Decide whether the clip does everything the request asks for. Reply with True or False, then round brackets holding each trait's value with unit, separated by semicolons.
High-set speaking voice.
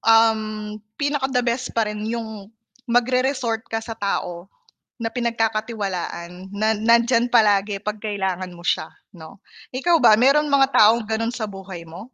True (225 Hz)